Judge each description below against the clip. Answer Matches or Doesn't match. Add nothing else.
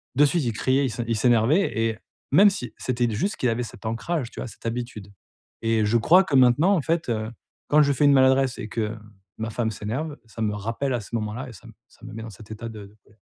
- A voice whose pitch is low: Matches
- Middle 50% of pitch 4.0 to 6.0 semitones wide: Doesn't match